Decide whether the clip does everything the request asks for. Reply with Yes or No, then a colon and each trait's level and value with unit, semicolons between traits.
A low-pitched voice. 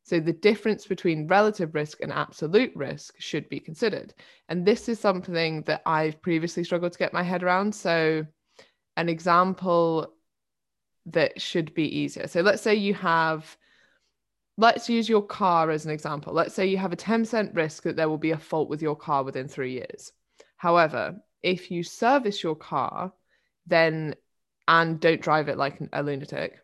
No: medium, 170 Hz